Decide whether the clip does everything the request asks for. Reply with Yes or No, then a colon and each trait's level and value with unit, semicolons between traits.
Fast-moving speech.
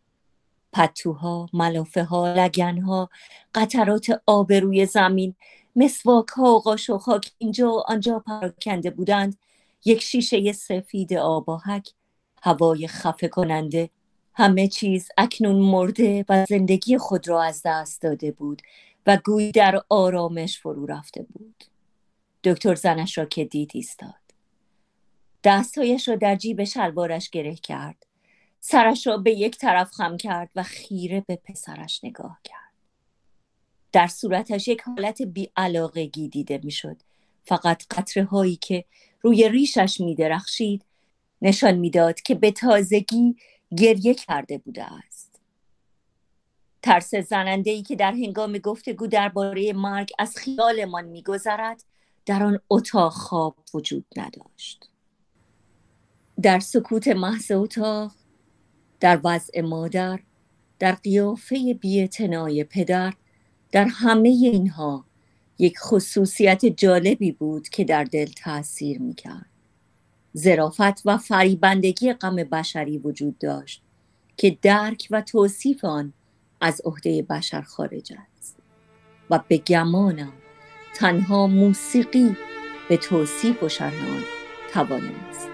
No: average, 115 wpm